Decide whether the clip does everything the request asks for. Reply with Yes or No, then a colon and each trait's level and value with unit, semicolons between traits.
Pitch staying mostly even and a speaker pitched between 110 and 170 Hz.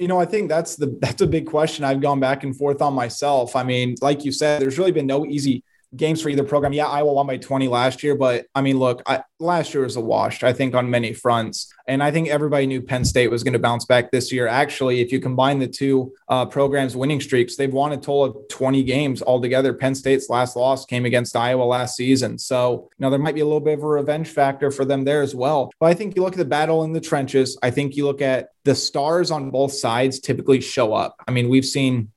Yes: narrow, 2.3 semitones; low, 135 Hz